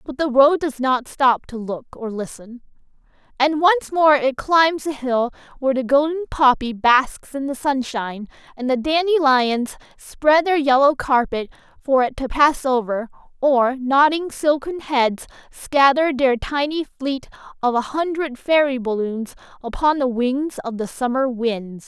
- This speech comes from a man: No, female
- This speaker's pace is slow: No, average, 155 wpm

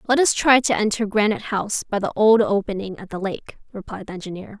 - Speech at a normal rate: No, fast, 220 wpm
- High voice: Yes, high, 210 Hz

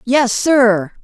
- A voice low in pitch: No, high, 240 Hz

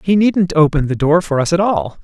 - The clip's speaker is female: No, male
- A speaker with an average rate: No, fast, 265 wpm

